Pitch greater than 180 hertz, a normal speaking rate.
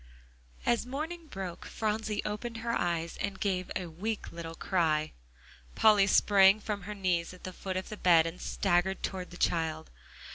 Yes: high, 190 Hz; average, 170 wpm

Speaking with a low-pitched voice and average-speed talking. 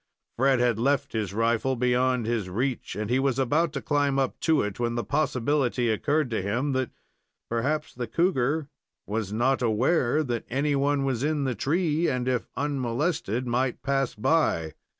Yes: low, 130 Hz; average, 170 wpm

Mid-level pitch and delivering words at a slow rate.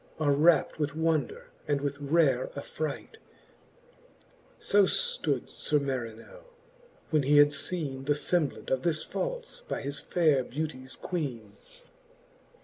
Yes: medium, 150 Hz; slow, 130 wpm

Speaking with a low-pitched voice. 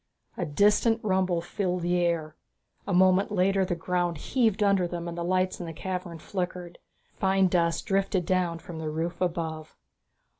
No: medium, 180 Hz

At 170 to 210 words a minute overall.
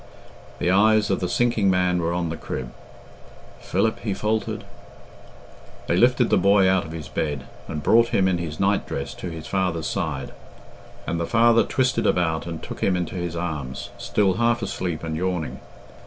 Yes: average, 180 wpm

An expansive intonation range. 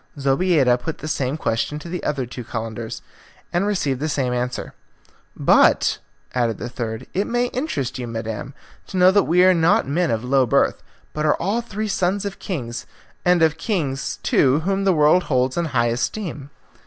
Yes: wide, 6.5 semitones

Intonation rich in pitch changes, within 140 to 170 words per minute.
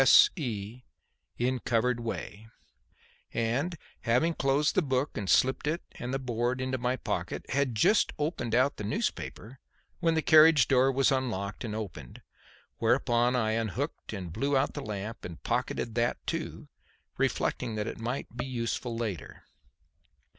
No: average, 3.3 semitones; average, 150 wpm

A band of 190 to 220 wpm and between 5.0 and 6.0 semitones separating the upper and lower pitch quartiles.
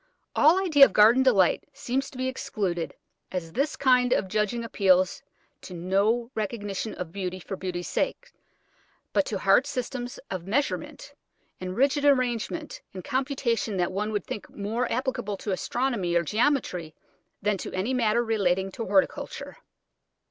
No: average, 150 wpm; wide, 5.4 semitones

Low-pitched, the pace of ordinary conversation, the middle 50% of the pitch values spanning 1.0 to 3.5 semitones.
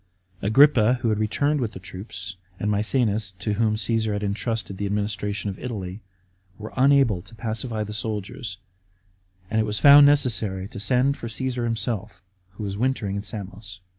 Yes: low, 110 Hz; average, 165 wpm; average, 2.9 semitones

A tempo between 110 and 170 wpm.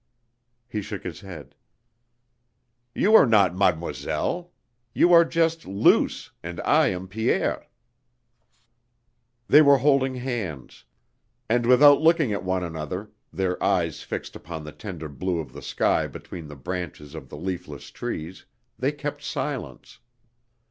Yes: slow, 135 wpm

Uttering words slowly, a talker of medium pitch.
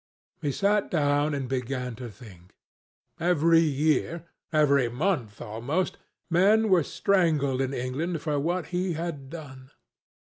Yes: slow, 115 wpm; medium, 150 Hz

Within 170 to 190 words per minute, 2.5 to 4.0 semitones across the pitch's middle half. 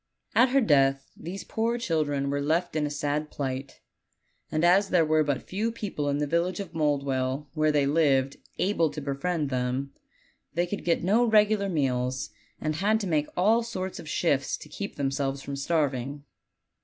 No: average, 180 wpm; average, 4.8 semitones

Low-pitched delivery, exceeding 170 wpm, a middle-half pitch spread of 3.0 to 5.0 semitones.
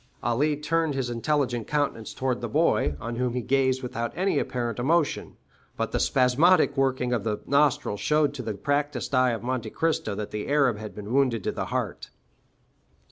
Yes: low, 130 Hz; average, 185 wpm; average, 3.5 semitones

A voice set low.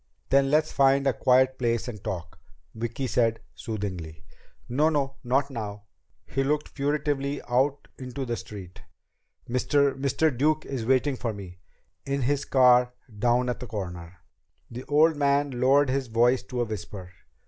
Yes: low, 130 Hz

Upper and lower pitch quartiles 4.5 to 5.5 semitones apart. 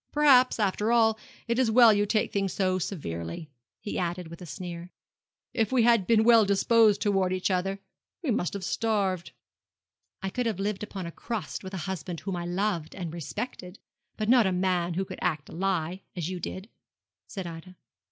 No: average, 3.6 semitones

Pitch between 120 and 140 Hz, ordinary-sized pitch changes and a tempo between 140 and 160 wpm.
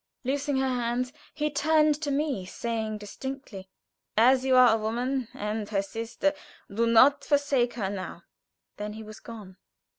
No: high, 240 Hz; average, 4.2 semitones; average, 155 wpm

